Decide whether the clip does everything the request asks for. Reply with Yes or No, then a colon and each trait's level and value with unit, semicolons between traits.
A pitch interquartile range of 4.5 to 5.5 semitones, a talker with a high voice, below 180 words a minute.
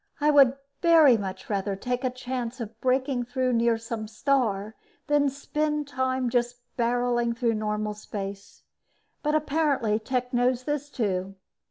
No: average, 3.7 semitones; high, 245 Hz; average, 140 wpm